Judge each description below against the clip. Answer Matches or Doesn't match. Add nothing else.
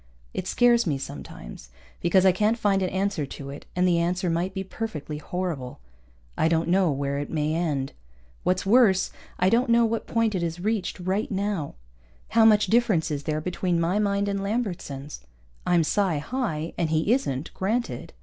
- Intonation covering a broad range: Doesn't match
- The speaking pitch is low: Doesn't match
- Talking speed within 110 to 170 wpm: Doesn't match